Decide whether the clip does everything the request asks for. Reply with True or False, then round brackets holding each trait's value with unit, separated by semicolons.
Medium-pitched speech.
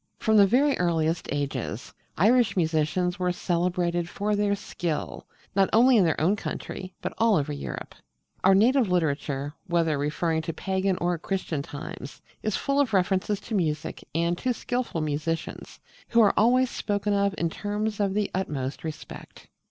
True (180 Hz)